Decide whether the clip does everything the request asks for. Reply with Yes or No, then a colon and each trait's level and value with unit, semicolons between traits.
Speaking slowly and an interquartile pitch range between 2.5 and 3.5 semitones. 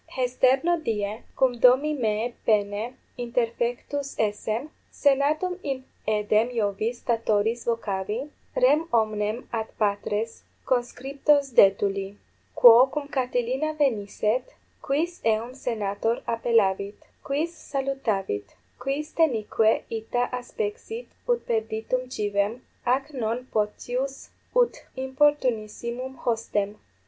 No: slow, 95 wpm; average, 4.1 semitones